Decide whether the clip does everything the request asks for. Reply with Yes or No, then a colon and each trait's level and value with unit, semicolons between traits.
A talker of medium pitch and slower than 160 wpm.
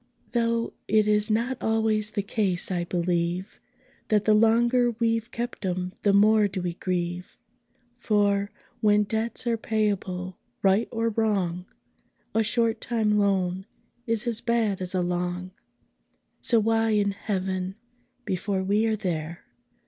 No: high, 210 Hz; average, 140 wpm